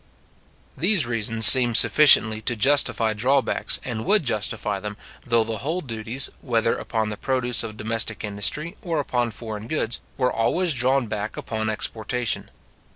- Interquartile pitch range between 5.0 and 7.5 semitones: No, average, 3.2 semitones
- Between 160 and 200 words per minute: No, average, 150 wpm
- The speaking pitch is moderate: No, low, 115 Hz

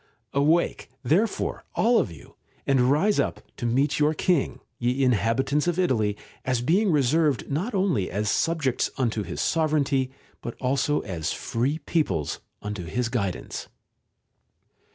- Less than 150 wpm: Yes, slow, 135 wpm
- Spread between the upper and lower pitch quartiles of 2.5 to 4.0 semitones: No, average, 5.2 semitones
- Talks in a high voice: No, low, 135 Hz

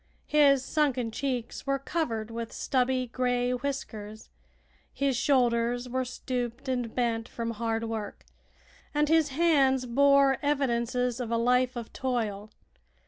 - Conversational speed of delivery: No, slow, 130 wpm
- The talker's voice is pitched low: No, very high, 250 Hz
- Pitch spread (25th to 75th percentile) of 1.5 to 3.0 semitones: Yes, average, 2.7 semitones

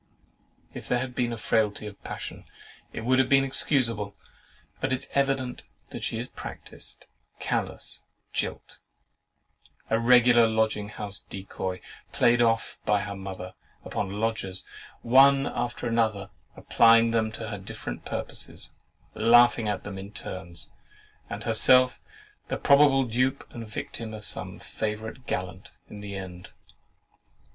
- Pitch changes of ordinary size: Yes, average, 3.2 semitones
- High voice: No, low, 110 Hz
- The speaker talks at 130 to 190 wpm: Yes, average, 140 wpm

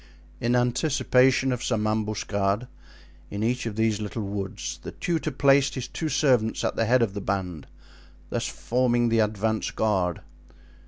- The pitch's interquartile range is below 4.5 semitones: Yes, average, 3.4 semitones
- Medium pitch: No, low, 115 Hz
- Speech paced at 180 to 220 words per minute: No, average, 155 wpm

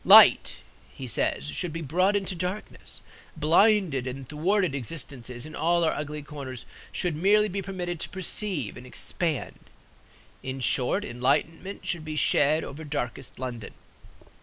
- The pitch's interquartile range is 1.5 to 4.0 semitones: No, wide, 5.5 semitones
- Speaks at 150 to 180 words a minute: No, average, 140 wpm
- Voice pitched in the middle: Yes, medium, 155 Hz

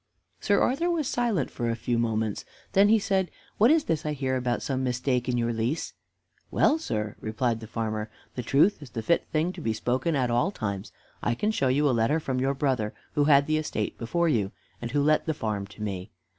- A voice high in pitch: No, low, 130 Hz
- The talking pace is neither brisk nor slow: No, fast, 225 wpm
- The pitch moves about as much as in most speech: No, wide, 5.7 semitones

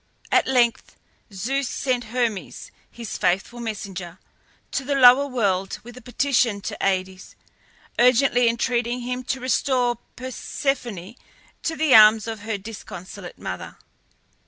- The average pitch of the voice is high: Yes, high, 240 Hz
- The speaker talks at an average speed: No, slow, 125 wpm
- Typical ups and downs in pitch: Yes, average, 3.6 semitones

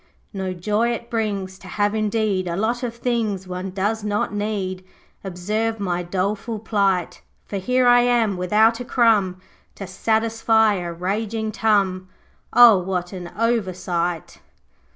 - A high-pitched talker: Yes, high, 205 Hz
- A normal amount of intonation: Yes, average, 3.2 semitones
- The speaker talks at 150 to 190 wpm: No, average, 140 wpm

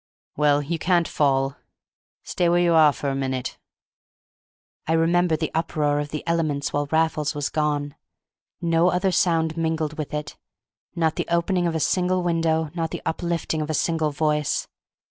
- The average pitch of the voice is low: No, medium, 160 Hz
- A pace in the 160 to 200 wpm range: Yes, average, 165 wpm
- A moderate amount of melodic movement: No, narrow, 2.2 semitones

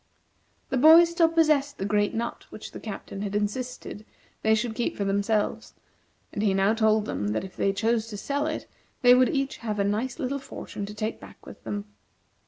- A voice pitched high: Yes, high, 220 Hz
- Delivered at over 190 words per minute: Yes, average, 200 wpm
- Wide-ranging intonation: No, average, 4.2 semitones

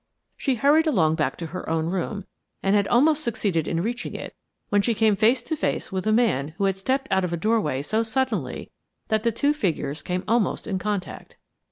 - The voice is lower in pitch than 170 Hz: No, high, 210 Hz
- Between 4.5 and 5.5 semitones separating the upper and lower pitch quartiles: Yes, average, 4.8 semitones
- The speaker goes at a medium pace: No, fast, 210 wpm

